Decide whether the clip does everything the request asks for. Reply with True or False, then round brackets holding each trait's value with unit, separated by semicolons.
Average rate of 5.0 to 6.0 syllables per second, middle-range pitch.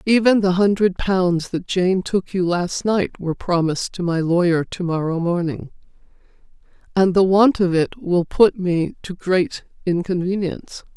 False (4.5 syllables/s; 180 Hz)